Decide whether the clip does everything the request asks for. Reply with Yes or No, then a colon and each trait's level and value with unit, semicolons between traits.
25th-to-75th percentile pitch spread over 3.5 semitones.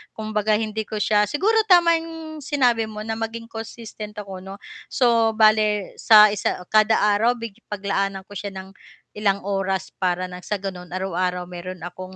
No: average, 2.8 semitones